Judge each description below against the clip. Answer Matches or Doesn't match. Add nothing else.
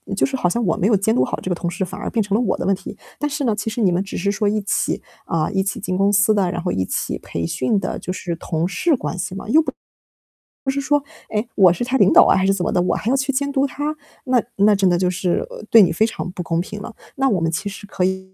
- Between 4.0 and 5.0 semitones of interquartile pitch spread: Matches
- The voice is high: Matches